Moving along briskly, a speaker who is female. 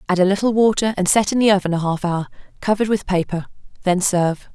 Yes: fast, 225 wpm; female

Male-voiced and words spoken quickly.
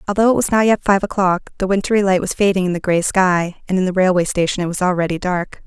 No: female; fast, 265 wpm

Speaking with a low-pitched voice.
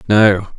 Yes: low, 100 Hz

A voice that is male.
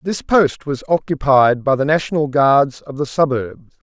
Yes: male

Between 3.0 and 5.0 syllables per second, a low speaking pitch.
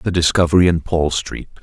No: 5.4 syllables/s; very low, 85 Hz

